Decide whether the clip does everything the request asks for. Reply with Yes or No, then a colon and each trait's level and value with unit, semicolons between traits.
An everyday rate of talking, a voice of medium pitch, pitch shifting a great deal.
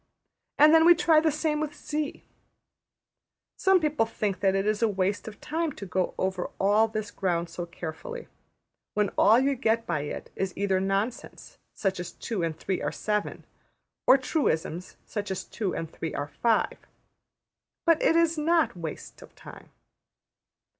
No: average, 165 wpm; high, 210 Hz; wide, 8.2 semitones